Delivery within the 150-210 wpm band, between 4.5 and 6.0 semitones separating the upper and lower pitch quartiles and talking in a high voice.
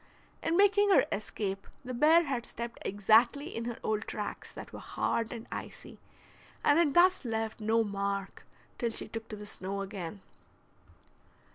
Yes: average, 160 wpm; wide, 5.5 semitones; high, 225 Hz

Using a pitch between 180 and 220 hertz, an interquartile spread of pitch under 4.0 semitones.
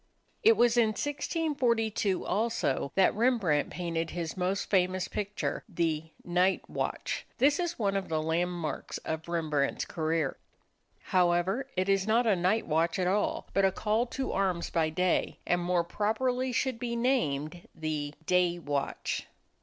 No: medium, 185 Hz; average, 5.2 semitones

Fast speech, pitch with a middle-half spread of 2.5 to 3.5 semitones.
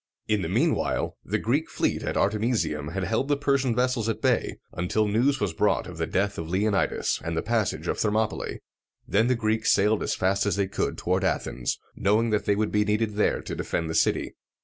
Yes: fast, 215 wpm; average, 2.9 semitones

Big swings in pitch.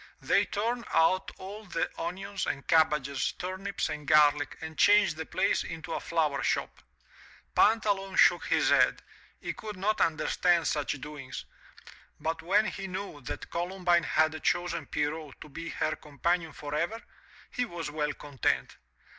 No: average, 4.3 semitones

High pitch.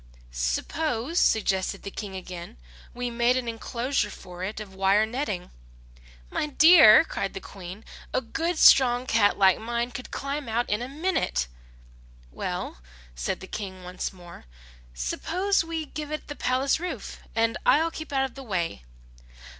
Yes: high, 230 Hz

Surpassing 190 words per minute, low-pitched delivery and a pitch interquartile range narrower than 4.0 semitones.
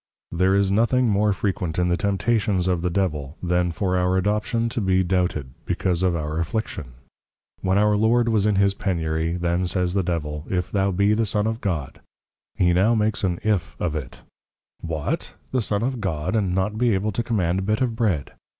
Yes: average, 200 wpm; very low, 95 Hz; average, 3.5 semitones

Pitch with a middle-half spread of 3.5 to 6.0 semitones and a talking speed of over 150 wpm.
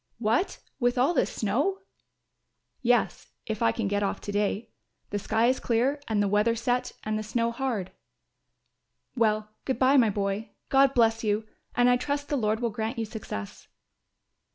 No: average, 2.8 semitones; average, 175 wpm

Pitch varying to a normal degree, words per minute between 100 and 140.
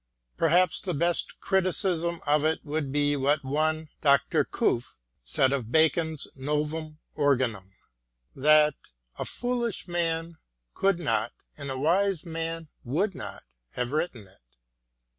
Yes: average, 3.5 semitones; slow, 135 wpm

